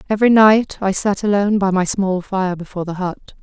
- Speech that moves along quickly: Yes, fast, 210 wpm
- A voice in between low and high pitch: No, high, 195 Hz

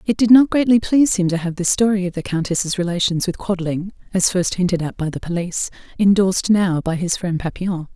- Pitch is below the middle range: No, medium, 185 Hz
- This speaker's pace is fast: Yes, fast, 220 wpm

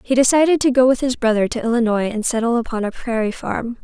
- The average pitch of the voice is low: No, high, 240 Hz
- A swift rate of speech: Yes, fast, 235 wpm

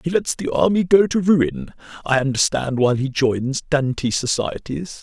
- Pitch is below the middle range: No, medium, 145 Hz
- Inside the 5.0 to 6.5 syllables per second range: No, 4.6 syllables/s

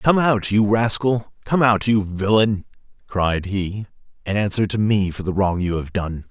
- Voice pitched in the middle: No, low, 100 Hz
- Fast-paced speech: No, average, 190 wpm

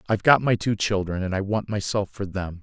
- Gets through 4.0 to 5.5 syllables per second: No, 5.7 syllables/s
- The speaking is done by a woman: No, male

